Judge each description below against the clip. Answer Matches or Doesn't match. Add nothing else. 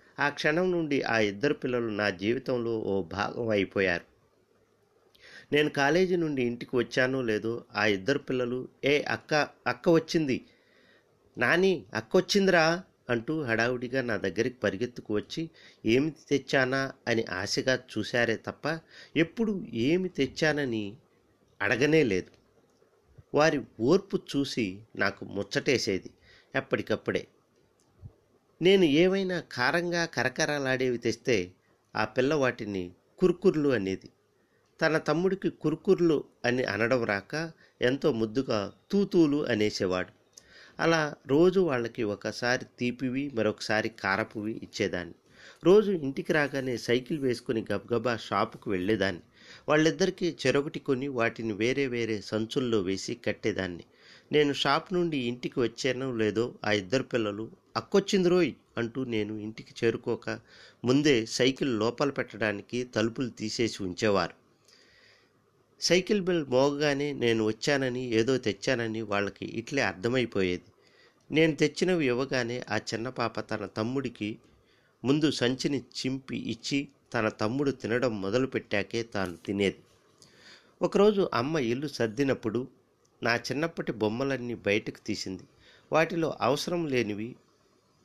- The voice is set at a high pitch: Doesn't match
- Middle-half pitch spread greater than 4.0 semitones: Matches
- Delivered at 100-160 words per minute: Matches